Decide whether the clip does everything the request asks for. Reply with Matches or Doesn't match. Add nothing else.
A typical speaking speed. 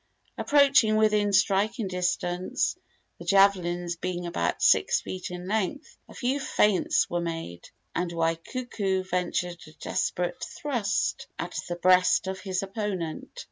Doesn't match